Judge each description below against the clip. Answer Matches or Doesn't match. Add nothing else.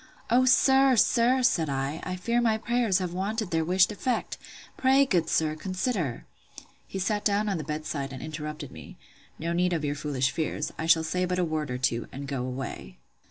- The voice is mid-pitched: Matches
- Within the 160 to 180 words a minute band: Doesn't match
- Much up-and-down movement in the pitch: Matches